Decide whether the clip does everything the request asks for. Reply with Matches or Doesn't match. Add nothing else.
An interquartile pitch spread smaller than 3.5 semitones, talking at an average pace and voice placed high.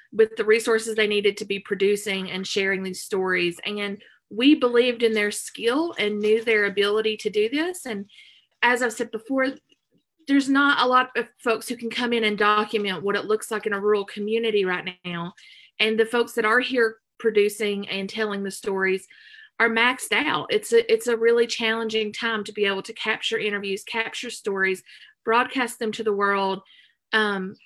Matches